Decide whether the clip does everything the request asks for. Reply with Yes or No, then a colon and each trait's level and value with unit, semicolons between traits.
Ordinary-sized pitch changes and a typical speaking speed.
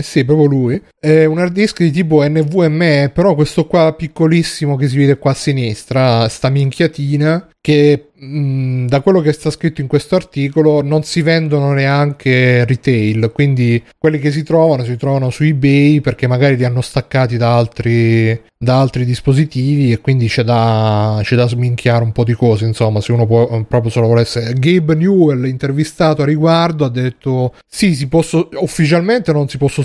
No: average, 4.2 semitones; fast, 175 wpm